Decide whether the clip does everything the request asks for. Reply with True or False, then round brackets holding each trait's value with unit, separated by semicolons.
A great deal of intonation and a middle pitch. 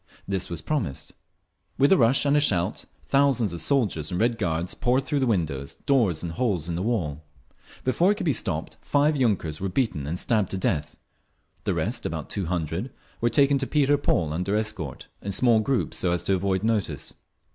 False (7.6 semitones; 100 Hz)